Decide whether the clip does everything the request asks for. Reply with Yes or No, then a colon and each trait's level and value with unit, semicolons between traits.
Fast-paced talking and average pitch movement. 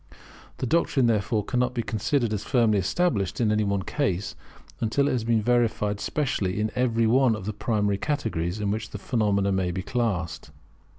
No: average, 175 wpm; average, 3.4 semitones